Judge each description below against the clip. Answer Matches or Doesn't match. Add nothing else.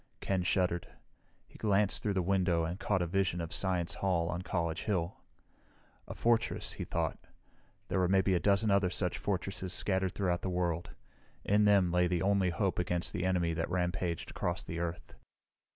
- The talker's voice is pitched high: Doesn't match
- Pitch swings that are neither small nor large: Doesn't match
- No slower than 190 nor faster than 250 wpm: Doesn't match